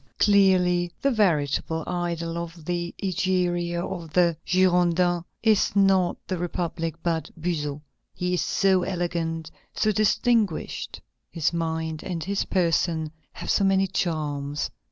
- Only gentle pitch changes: Yes, narrow, 2.3 semitones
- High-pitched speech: No, medium, 175 Hz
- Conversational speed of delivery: No, slow, 125 wpm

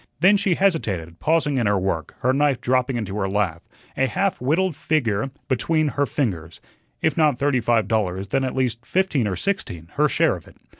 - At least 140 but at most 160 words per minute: No, average, 195 wpm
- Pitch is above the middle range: No, low, 125 Hz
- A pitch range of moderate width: No, wide, 7.3 semitones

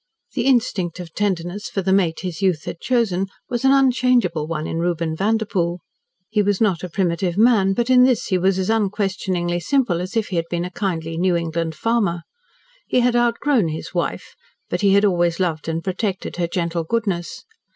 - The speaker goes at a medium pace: Yes, average, 195 wpm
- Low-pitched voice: No, high, 190 Hz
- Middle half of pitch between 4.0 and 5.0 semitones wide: Yes, average, 4.6 semitones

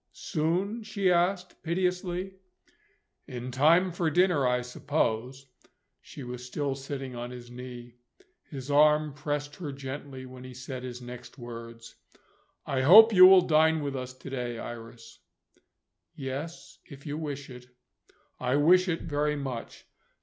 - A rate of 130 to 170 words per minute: Yes, average, 140 wpm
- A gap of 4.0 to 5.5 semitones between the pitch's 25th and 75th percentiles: Yes, average, 4.4 semitones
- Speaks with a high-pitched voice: No, medium, 140 Hz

